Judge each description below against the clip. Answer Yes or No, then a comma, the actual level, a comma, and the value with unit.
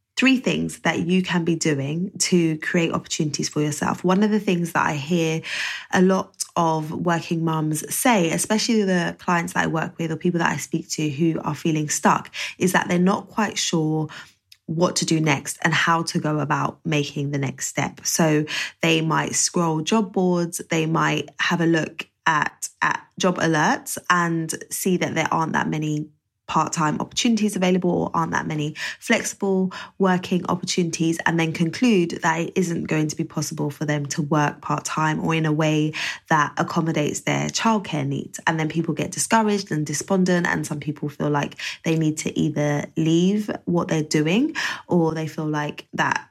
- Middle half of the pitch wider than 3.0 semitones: No, average, 2.7 semitones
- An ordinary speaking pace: Yes, average, 185 wpm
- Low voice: No, medium, 165 Hz